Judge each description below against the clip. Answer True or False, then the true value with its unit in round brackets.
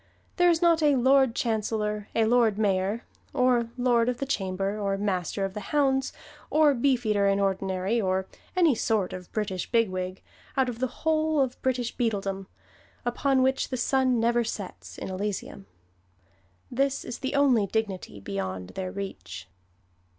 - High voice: True (225 Hz)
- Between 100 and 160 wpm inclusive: True (155 wpm)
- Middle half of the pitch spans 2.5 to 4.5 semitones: False (5.1 semitones)